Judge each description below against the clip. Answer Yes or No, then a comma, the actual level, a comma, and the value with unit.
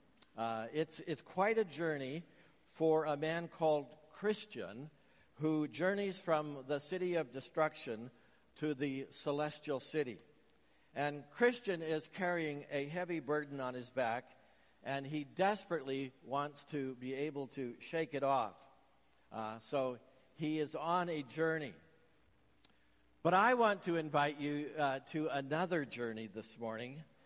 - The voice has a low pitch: No, medium, 150 Hz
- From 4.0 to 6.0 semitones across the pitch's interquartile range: No, average, 3.1 semitones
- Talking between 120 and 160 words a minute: Yes, slow, 135 wpm